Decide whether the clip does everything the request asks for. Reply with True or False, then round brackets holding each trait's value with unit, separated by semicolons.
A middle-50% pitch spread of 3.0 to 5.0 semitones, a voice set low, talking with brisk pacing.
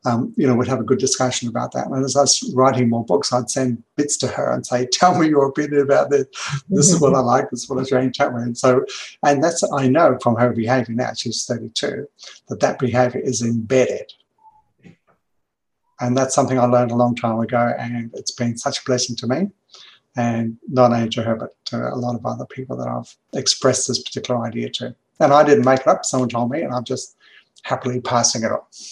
False (2.6 semitones; 125 Hz; 235 wpm)